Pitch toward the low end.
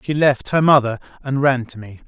Yes: low, 130 Hz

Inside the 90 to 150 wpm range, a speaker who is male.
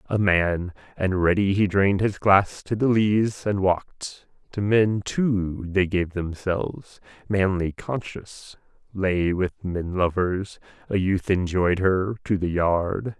Yes: average, 145 wpm; male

